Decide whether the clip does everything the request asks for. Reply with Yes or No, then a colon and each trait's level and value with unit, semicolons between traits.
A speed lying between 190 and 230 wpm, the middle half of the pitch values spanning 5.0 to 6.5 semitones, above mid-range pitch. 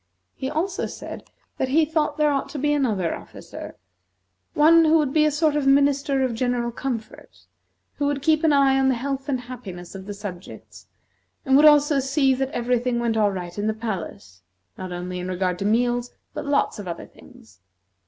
Yes: average, 200 wpm; wide, 5.5 semitones; very high, 260 Hz